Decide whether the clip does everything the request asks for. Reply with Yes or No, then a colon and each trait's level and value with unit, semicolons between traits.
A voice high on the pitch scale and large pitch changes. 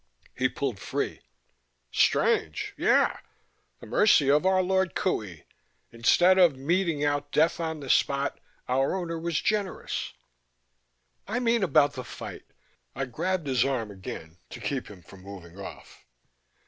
No: medium, 140 Hz; wide, 8.6 semitones